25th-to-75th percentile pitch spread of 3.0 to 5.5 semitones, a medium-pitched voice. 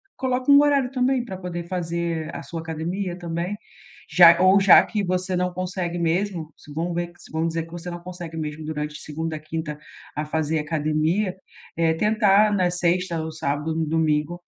No: narrow, 2.5 semitones; medium, 170 Hz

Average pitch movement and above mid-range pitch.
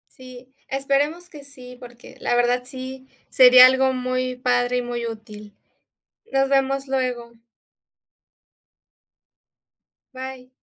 No: narrow, 1.4 semitones; very high, 255 Hz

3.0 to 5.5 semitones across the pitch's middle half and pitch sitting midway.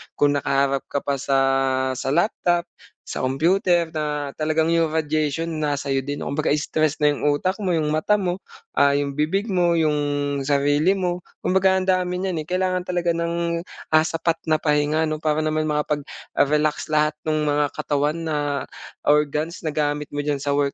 No: narrow, 2.6 semitones; medium, 155 Hz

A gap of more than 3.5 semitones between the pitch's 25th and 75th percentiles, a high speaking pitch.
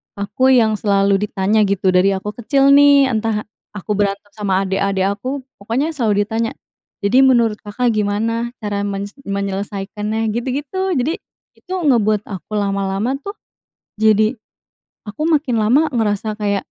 Yes: average, 3.9 semitones; high, 215 Hz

